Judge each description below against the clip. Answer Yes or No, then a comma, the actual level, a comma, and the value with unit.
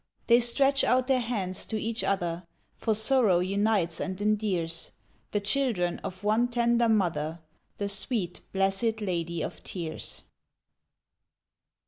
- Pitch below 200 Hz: No, high, 205 Hz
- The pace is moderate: No, slow, 125 wpm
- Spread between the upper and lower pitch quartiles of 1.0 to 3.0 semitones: No, average, 4.6 semitones